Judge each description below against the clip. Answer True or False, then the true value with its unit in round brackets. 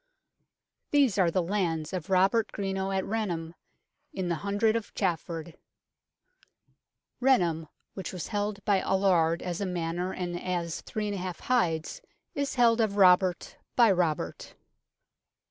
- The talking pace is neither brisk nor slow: False (130 wpm)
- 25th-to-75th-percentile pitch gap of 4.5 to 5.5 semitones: False (3.2 semitones)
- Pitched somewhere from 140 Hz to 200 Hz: True (185 Hz)